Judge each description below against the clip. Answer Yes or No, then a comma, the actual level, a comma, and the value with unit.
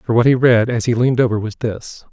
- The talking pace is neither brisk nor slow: No, fast, 285 wpm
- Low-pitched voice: Yes, low, 120 Hz